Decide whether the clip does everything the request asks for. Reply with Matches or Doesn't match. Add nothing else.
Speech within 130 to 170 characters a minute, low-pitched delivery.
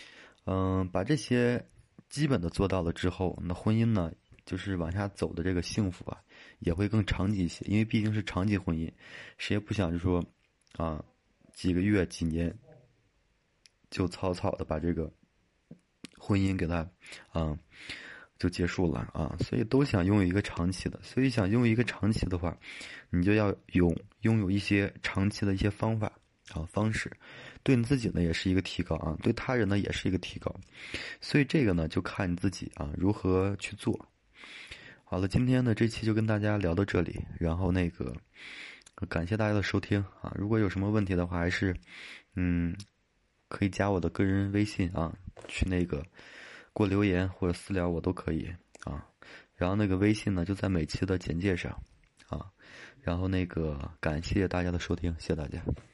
Doesn't match